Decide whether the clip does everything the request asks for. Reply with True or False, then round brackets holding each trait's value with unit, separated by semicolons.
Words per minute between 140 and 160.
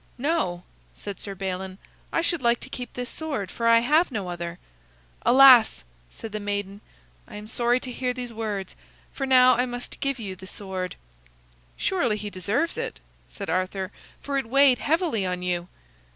False (175 wpm)